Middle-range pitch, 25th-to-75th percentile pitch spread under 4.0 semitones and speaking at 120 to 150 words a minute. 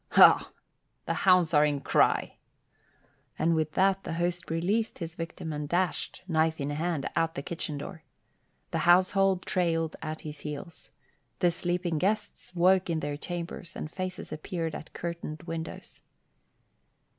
Yes: medium, 170 Hz; narrow, 2.5 semitones; average, 145 wpm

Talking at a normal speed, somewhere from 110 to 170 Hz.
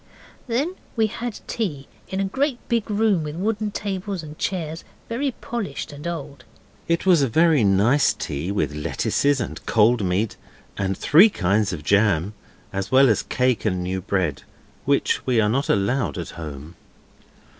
Yes: average, 165 wpm; medium, 140 Hz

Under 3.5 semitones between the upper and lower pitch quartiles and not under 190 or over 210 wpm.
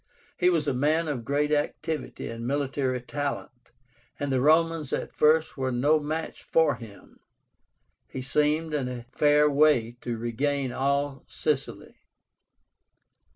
No: average, 3.0 semitones; slow, 135 wpm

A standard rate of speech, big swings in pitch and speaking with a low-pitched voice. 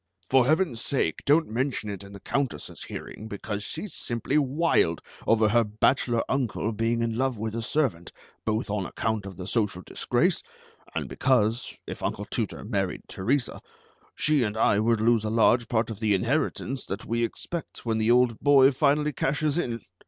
No: average, 175 wpm; average, 3.8 semitones; low, 115 Hz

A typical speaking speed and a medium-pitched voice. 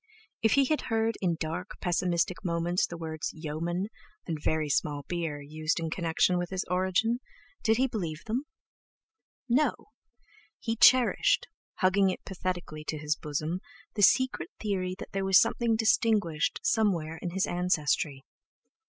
Yes: average, 145 wpm; medium, 180 Hz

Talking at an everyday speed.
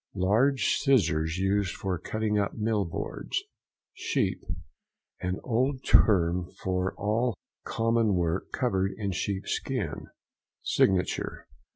No: slow, 100 wpm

